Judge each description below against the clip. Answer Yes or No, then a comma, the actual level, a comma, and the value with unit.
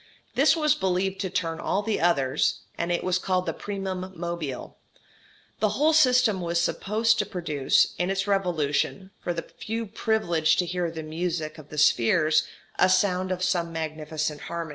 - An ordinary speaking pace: Yes, average, 170 wpm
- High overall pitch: No, medium, 180 Hz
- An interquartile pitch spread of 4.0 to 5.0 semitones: No, average, 3.3 semitones